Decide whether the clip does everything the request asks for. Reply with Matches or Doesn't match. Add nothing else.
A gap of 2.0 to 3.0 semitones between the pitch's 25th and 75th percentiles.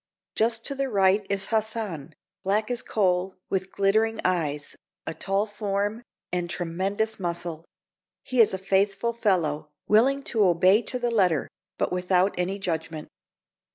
Doesn't match